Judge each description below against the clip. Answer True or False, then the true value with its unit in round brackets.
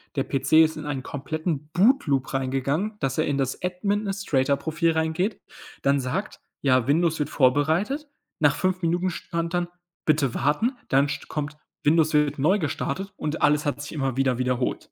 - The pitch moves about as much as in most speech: True (4.0 semitones)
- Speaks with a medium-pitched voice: True (150 Hz)